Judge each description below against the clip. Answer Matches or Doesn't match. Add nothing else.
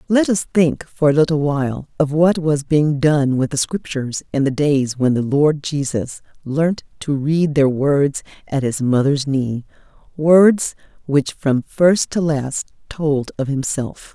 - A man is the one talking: Doesn't match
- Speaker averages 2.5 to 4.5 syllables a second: Matches